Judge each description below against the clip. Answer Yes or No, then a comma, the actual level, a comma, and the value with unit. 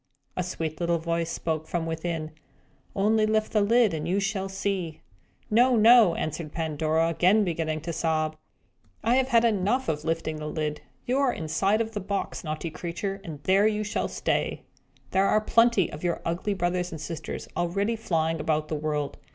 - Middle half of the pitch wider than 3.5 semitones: Yes, average, 4.9 semitones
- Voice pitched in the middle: Yes, medium, 175 Hz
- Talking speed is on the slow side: No, average, 180 wpm